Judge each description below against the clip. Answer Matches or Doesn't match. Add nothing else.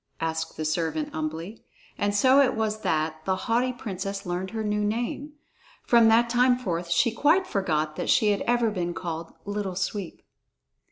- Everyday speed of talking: Matches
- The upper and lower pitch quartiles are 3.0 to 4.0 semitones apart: Doesn't match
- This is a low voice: Doesn't match